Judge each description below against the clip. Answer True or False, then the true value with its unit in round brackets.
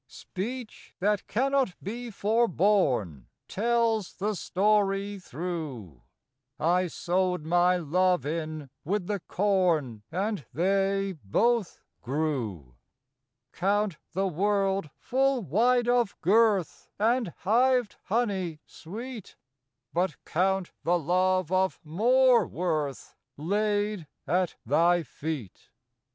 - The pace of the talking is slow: True (100 wpm)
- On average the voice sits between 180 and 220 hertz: True (190 Hz)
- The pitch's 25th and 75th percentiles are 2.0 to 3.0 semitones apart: False (4.4 semitones)